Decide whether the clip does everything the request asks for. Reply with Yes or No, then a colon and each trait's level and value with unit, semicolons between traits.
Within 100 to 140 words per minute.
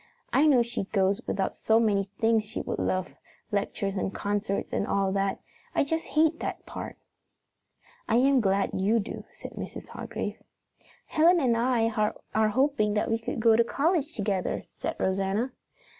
No: average, 165 wpm